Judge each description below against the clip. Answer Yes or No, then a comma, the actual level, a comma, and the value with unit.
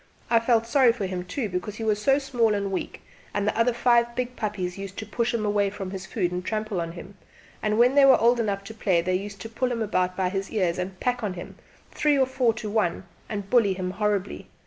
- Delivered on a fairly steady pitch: No, average, 3.6 semitones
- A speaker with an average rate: No, fast, 250 wpm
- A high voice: Yes, high, 210 Hz